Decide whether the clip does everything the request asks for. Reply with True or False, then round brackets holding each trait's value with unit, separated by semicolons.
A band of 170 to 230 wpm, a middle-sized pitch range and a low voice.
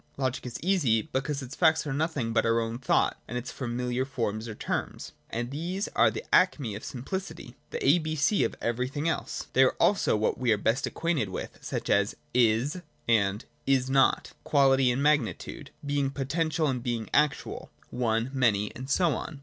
True (190 wpm; 4.3 semitones; 130 Hz)